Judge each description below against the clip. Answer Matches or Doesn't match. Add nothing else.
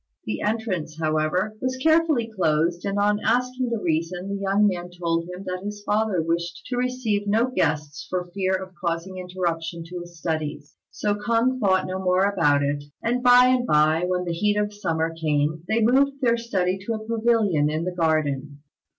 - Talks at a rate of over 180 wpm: Matches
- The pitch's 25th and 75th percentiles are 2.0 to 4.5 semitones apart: Doesn't match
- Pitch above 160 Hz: Matches